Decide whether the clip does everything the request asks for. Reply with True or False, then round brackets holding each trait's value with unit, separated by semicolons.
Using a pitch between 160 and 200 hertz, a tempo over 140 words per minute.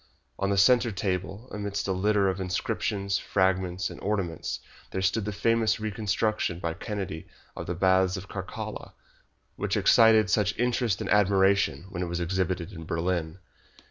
False (95 Hz; 155 wpm)